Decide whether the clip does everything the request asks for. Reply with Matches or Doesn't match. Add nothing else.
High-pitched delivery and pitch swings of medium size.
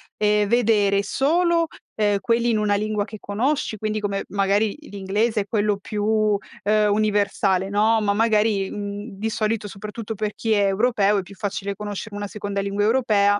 Doesn't match